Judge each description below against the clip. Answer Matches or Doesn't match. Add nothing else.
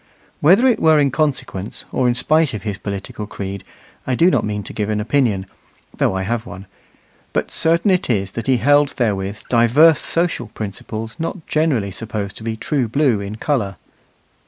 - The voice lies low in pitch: Matches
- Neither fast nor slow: Matches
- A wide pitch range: Matches